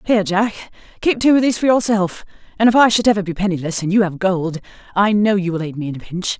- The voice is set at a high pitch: Yes, high, 195 Hz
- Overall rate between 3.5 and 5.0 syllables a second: No, 6.4 syllables/s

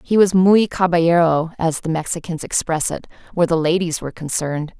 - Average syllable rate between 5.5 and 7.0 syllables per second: Yes, 5.7 syllables/s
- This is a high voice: No, medium, 170 Hz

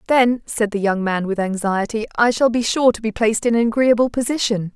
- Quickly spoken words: Yes, fast, 225 wpm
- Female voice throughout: Yes, female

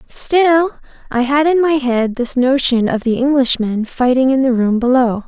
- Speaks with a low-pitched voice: No, very high, 260 Hz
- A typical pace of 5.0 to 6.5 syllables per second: No, 4.4 syllables/s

